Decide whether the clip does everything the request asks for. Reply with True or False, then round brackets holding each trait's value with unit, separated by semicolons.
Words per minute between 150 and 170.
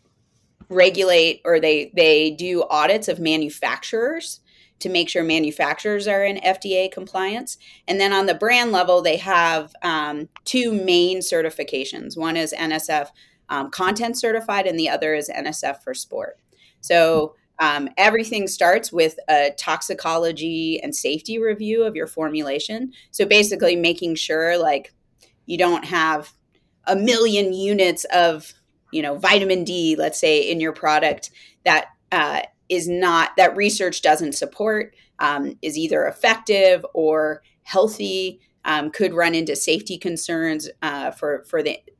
False (140 wpm)